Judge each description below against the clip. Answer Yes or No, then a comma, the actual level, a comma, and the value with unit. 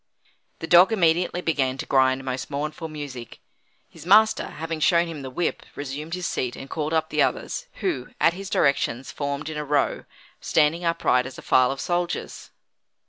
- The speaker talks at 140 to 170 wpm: No, average, 180 wpm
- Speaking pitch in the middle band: Yes, medium, 155 Hz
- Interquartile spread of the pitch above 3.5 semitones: Yes, average, 4.0 semitones